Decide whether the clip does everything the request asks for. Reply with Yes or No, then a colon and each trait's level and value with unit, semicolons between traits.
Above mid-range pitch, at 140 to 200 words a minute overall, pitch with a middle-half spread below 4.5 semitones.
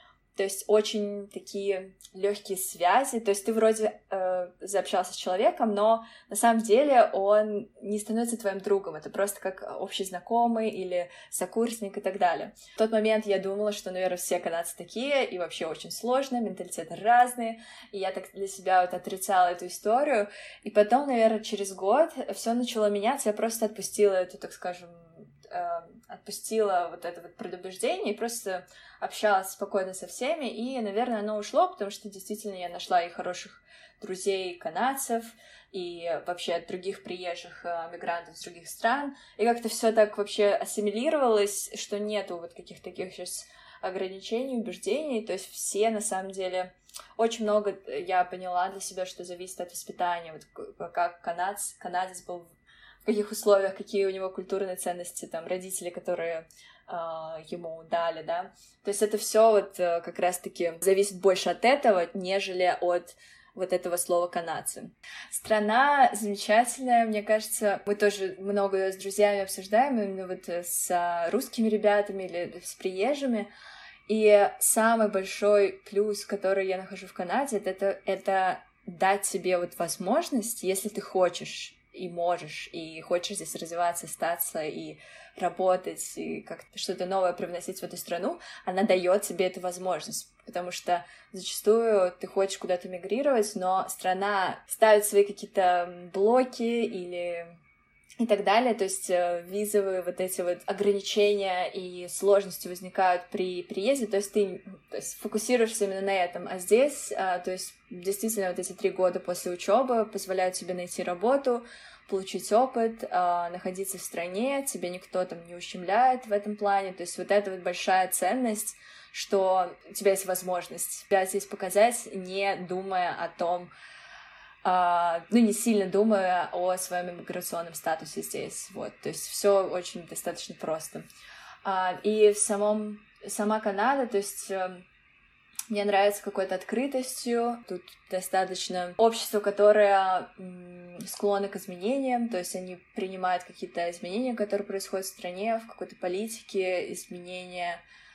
Yes: high, 195 Hz; average, 150 wpm; average, 2.9 semitones